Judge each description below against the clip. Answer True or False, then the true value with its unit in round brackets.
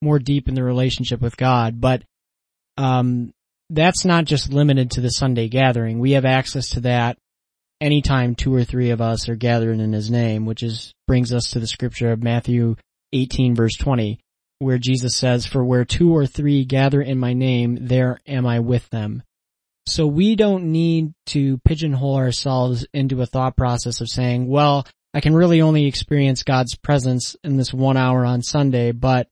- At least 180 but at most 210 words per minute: True (185 wpm)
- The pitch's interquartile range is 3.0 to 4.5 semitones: False (2.4 semitones)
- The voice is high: False (130 Hz)